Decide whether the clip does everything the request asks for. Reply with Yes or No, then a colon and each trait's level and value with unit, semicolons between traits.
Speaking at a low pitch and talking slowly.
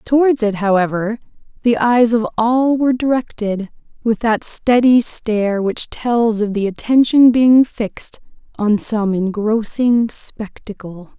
No: high, 225 Hz; slow, 130 wpm